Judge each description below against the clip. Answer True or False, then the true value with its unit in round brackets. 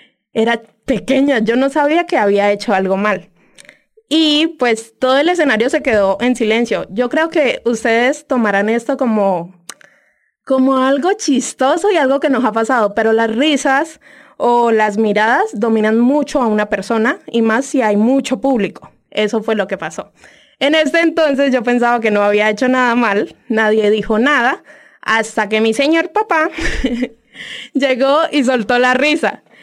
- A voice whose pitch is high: True (245 Hz)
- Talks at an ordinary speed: True (165 wpm)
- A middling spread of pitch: True (4.2 semitones)